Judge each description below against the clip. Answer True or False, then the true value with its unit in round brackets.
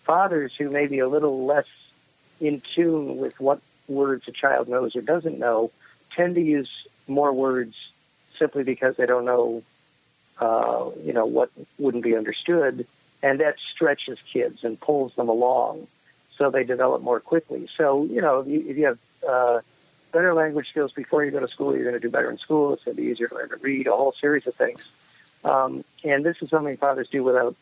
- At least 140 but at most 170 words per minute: False (200 wpm)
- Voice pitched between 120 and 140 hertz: True (135 Hz)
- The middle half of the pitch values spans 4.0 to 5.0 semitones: False (3.0 semitones)